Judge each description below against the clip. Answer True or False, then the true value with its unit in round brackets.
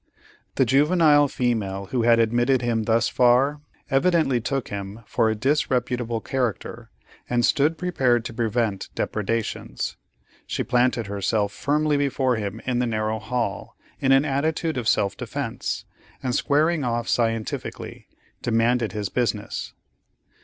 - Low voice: True (120 Hz)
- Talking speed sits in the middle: False (130 wpm)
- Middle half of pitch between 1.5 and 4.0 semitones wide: True (3.4 semitones)